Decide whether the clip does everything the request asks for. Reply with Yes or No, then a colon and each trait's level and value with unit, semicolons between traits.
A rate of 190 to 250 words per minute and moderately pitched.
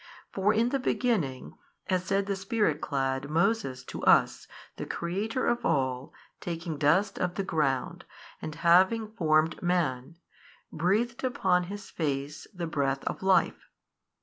No: average, 140 wpm; medium, 175 Hz